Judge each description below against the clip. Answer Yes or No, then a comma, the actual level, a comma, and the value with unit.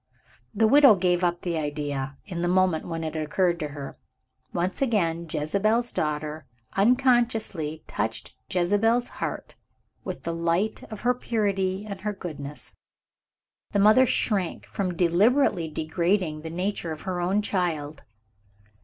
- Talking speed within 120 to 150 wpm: Yes, slow, 135 wpm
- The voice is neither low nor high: Yes, medium, 180 Hz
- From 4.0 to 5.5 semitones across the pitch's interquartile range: Yes, average, 4.7 semitones